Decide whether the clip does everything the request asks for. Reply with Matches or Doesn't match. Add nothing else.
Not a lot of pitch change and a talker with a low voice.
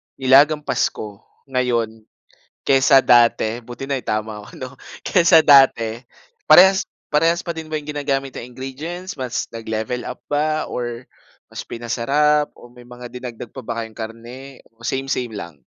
Doesn't match